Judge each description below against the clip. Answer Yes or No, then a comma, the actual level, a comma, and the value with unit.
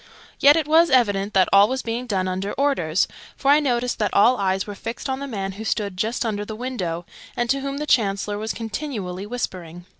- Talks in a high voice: Yes, high, 220 Hz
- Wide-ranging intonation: No, average, 4.9 semitones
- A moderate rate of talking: No, fast, 215 wpm